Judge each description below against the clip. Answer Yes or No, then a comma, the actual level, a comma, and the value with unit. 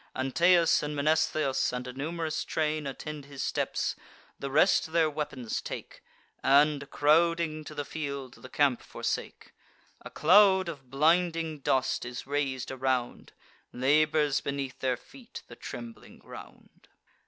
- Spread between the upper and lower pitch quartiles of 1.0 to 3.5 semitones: Yes, average, 3.0 semitones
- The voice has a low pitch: No, medium, 150 Hz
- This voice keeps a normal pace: No, slow, 130 wpm